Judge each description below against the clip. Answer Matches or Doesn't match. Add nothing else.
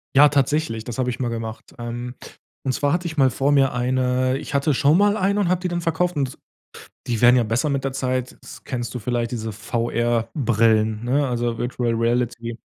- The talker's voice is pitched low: Matches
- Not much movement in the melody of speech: Doesn't match